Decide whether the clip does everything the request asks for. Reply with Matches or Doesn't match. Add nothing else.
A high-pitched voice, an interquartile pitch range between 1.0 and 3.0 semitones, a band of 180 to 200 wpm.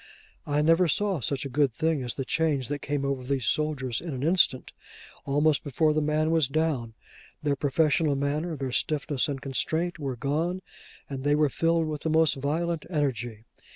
Doesn't match